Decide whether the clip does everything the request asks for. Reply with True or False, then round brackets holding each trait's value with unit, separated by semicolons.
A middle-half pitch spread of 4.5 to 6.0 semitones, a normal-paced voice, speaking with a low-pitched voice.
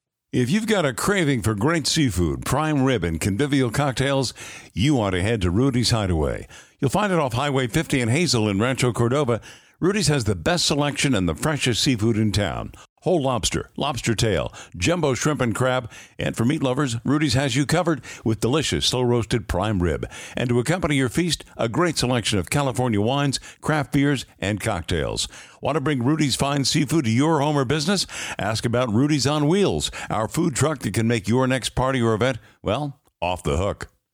True (4.8 semitones; 195 wpm; 130 Hz)